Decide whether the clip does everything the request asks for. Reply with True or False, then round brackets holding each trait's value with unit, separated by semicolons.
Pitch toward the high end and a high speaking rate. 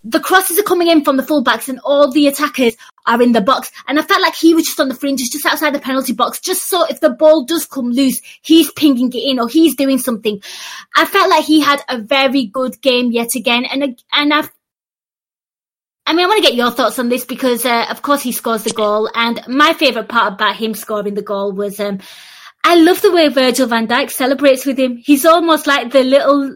True (270 Hz; 235 wpm)